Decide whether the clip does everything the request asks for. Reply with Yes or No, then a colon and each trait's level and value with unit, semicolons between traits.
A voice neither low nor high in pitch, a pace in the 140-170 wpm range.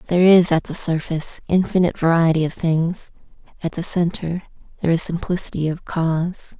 Yes: medium, 170 Hz; average, 155 wpm